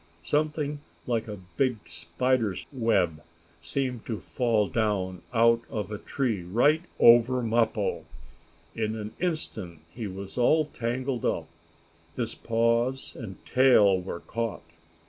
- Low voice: Yes, low, 115 Hz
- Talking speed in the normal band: No, slow, 125 wpm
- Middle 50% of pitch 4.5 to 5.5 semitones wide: No, average, 3.9 semitones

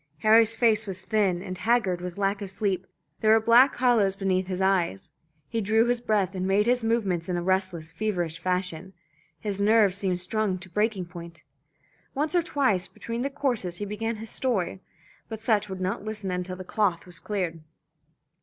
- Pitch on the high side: Yes, high, 195 Hz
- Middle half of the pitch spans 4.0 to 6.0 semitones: No, average, 3.3 semitones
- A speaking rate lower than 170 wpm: No, average, 185 wpm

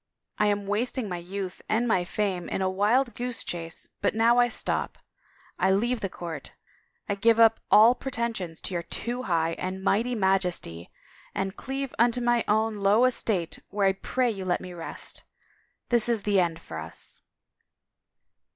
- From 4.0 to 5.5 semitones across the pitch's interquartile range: Yes, average, 4.3 semitones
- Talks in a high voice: Yes, high, 205 Hz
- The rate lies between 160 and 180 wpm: Yes, average, 170 wpm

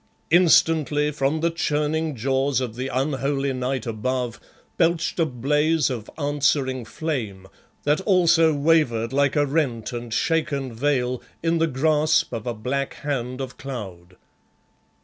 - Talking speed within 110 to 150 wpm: Yes, slow, 135 wpm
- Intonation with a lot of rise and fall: No, average, 3.8 semitones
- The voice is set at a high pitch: No, medium, 140 Hz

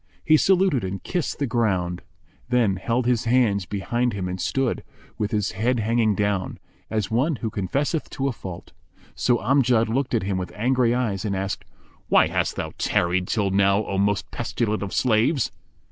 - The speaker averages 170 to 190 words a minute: Yes, average, 175 wpm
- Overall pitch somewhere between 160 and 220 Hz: No, low, 110 Hz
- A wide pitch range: No, average, 4.2 semitones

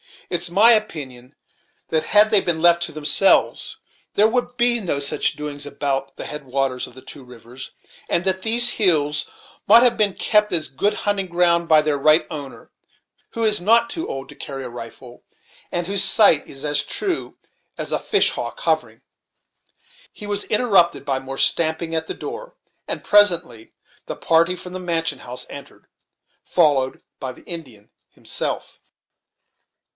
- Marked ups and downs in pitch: Yes, wide, 6.7 semitones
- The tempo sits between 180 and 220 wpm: No, average, 170 wpm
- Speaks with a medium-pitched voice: Yes, medium, 170 Hz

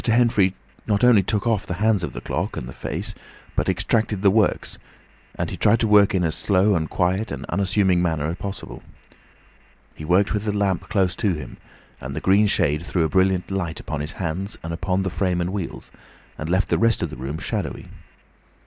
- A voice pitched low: Yes, very low, 95 Hz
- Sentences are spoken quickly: Yes, fast, 210 wpm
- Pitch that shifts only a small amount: No, average, 3.2 semitones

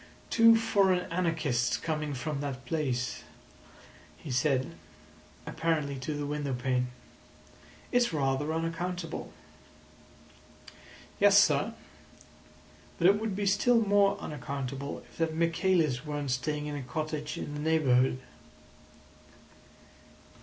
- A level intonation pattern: No, average, 4.5 semitones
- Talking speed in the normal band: No, slow, 110 wpm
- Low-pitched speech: No, medium, 155 Hz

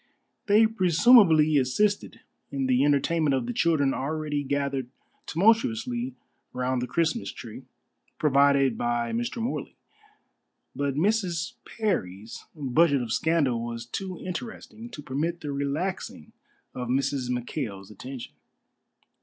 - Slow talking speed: Yes, slow, 115 wpm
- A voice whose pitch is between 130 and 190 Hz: Yes, medium, 140 Hz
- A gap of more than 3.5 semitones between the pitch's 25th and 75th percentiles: Yes, average, 5.1 semitones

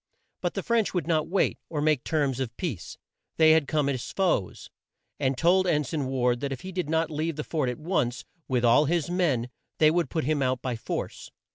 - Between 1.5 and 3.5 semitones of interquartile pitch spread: No, average, 4.1 semitones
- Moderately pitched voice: Yes, medium, 150 Hz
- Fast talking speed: Yes, fast, 220 wpm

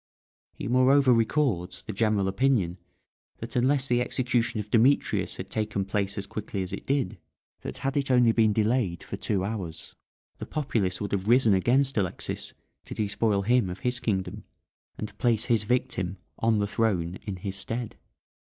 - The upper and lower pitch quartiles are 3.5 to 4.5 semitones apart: Yes, average, 4.0 semitones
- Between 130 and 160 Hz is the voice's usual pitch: No, low, 110 Hz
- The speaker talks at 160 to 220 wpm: Yes, average, 170 wpm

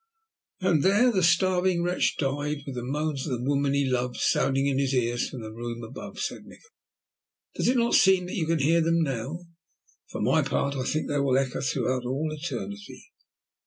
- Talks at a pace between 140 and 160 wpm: No, average, 200 wpm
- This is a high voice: No, medium, 140 Hz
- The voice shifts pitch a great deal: No, average, 4.6 semitones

